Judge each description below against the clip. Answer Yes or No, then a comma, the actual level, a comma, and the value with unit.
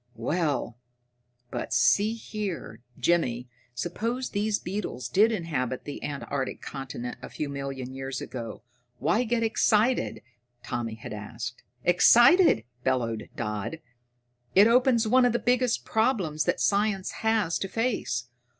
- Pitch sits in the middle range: Yes, medium, 175 Hz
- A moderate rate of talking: No, slow, 125 wpm